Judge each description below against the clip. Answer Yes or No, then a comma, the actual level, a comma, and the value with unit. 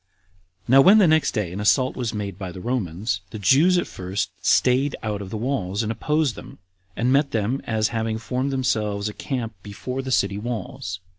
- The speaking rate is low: No, fast, 205 wpm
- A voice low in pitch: Yes, low, 115 Hz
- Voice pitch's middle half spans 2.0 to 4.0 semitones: No, average, 4.5 semitones